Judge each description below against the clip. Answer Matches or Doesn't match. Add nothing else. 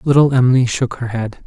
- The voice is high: Doesn't match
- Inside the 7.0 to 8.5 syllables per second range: Doesn't match